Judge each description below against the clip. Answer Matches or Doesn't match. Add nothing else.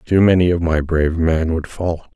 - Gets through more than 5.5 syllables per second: Doesn't match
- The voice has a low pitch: Matches